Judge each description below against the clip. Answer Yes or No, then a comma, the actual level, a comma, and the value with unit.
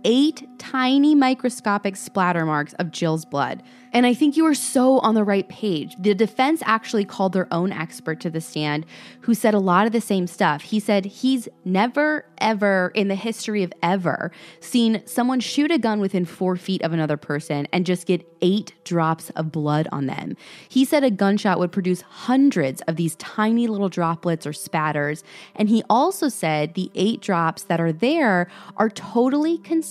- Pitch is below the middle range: No, high, 200 Hz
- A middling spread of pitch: No, wide, 6.1 semitones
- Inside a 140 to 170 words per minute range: No, average, 185 wpm